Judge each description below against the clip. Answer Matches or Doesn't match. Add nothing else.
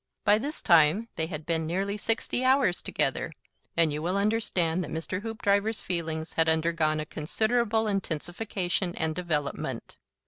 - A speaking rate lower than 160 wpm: Matches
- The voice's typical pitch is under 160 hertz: Doesn't match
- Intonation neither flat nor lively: Matches